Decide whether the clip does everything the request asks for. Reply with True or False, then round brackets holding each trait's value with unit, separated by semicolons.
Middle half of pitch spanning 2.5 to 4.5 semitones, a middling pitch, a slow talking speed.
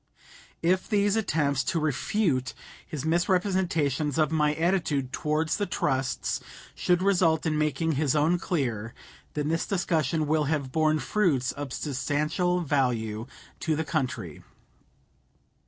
True (3.6 semitones; 155 Hz; 125 wpm)